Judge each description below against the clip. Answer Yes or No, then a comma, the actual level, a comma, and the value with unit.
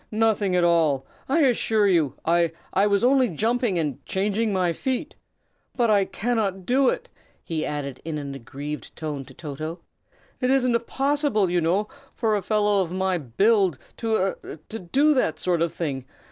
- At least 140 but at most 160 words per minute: No, average, 170 wpm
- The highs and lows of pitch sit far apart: Yes, wide, 5.8 semitones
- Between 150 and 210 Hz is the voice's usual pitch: Yes, high, 190 Hz